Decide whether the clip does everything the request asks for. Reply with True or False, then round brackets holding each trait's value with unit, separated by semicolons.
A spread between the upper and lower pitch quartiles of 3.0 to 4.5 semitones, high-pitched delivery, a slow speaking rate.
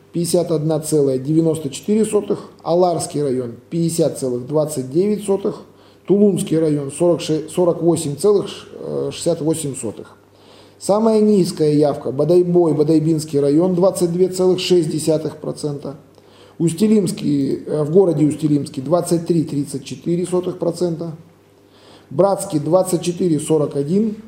False (3.8 semitones; 160 Hz; 50 wpm)